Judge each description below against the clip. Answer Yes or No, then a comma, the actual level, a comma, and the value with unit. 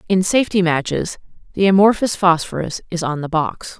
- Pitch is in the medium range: Yes, medium, 180 Hz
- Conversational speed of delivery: Yes, average, 160 wpm